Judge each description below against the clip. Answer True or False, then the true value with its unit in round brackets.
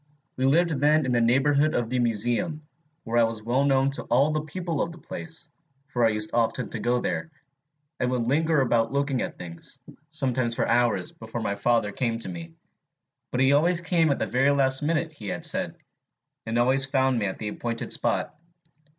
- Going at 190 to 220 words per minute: True (200 wpm)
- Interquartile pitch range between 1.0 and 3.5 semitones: False (4.2 semitones)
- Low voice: True (130 Hz)